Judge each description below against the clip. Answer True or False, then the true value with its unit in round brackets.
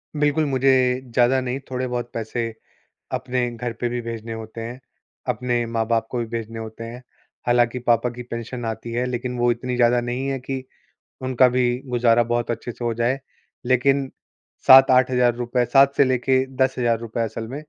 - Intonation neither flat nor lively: False (1.6 semitones)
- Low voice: True (120 Hz)